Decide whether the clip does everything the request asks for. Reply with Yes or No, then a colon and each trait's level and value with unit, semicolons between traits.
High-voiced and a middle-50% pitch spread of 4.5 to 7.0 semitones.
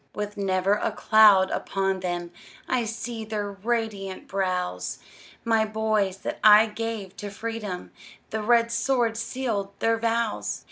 No: high, 215 Hz; average, 2.7 semitones